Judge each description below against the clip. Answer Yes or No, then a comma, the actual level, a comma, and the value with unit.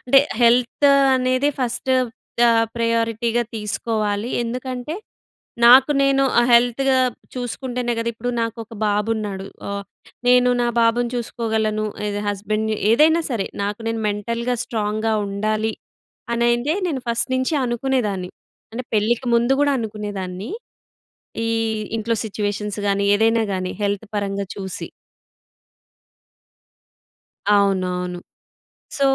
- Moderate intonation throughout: Yes, average, 3.0 semitones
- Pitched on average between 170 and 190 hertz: No, high, 230 Hz